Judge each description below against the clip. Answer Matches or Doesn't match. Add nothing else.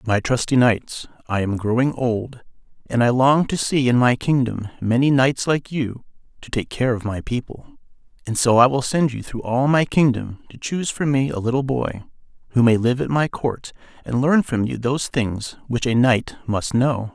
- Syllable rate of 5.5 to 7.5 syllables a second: Doesn't match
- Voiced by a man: Matches